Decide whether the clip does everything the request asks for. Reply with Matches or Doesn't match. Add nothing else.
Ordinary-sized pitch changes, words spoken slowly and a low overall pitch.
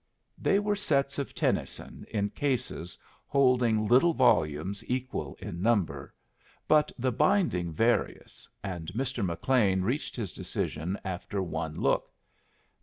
Doesn't match